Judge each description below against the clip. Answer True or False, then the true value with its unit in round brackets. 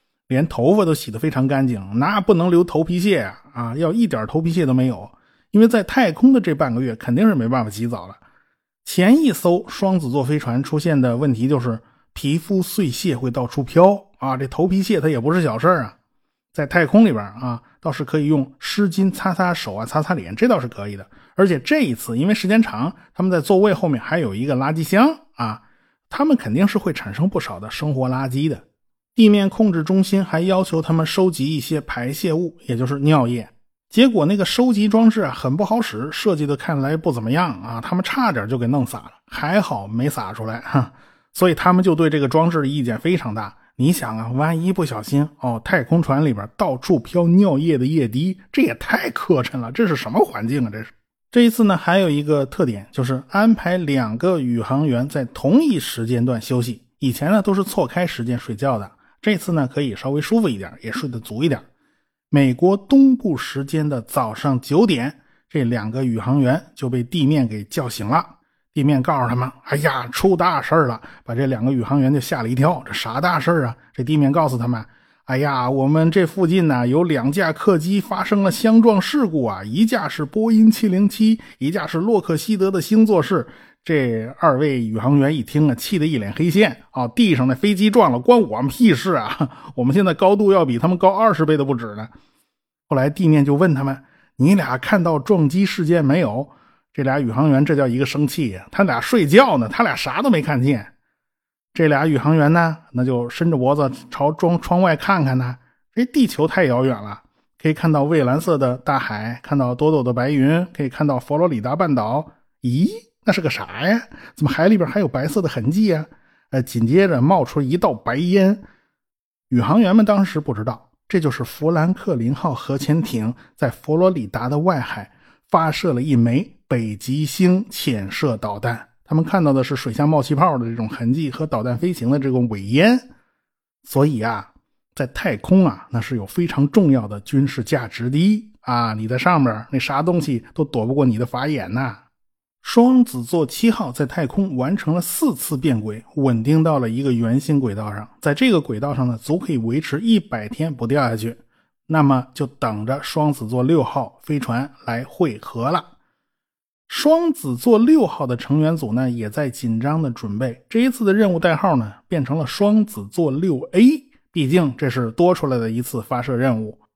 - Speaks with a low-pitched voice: False (150 Hz)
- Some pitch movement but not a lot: False (6.4 semitones)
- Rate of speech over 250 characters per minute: True (290 characters per minute)